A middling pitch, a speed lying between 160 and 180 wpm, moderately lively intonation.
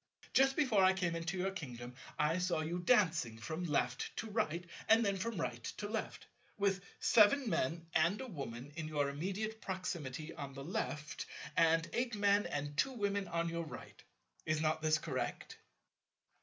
Yes: medium, 170 Hz; average, 170 wpm; average, 4.9 semitones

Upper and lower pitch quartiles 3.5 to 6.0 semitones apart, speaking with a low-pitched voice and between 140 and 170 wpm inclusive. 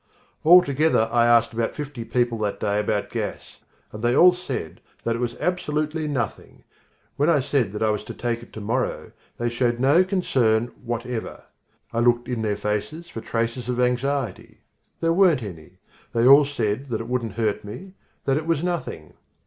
No: average, 4.4 semitones; low, 120 Hz; average, 180 wpm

